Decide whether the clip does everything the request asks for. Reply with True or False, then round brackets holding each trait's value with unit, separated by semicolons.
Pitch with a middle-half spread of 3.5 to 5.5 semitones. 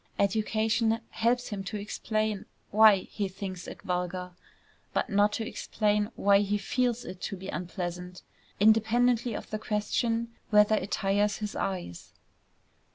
False (2.4 semitones)